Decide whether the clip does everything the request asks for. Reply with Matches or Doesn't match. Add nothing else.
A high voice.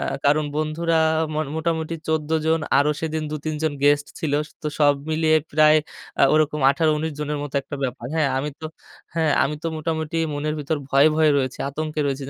Doesn't match